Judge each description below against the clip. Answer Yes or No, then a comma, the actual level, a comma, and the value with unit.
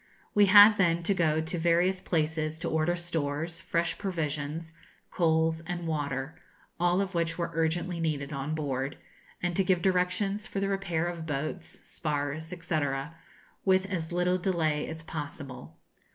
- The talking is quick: No, average, 150 wpm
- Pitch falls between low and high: Yes, medium, 165 Hz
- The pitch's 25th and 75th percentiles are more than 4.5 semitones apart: No, narrow, 2.5 semitones